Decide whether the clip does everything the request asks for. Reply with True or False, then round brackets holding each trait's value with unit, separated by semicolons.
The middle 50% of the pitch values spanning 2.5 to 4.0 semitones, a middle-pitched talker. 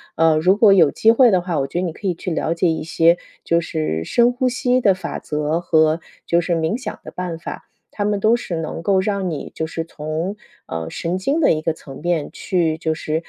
True (3.6 semitones; 170 Hz)